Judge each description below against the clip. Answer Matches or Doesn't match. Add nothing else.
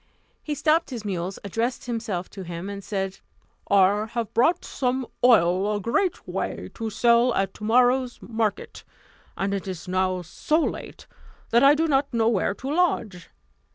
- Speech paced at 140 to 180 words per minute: Matches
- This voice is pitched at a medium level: Doesn't match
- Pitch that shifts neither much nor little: Matches